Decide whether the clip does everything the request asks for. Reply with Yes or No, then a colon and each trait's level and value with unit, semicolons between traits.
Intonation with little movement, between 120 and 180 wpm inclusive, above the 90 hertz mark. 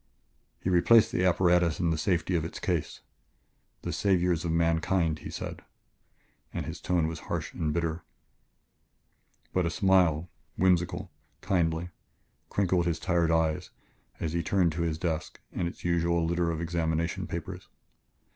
No: narrow, 1.5 semitones; average, 145 wpm; very low, 85 Hz